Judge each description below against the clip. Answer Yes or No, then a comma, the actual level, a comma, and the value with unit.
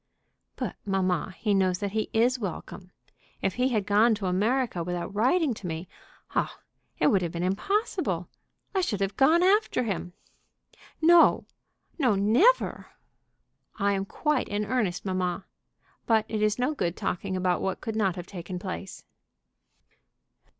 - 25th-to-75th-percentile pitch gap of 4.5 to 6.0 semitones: Yes, average, 4.9 semitones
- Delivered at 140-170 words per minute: Yes, average, 150 wpm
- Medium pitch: No, high, 205 Hz